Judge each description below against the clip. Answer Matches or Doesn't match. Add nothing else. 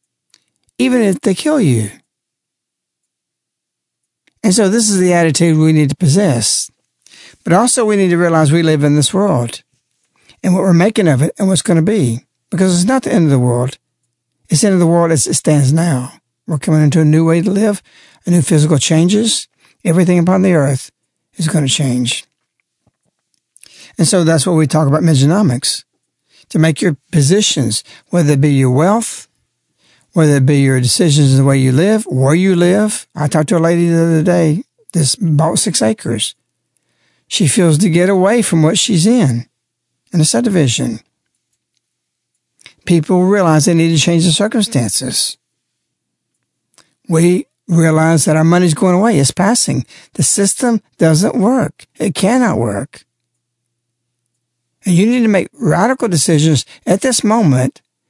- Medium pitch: Matches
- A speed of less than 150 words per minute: Doesn't match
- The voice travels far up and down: Doesn't match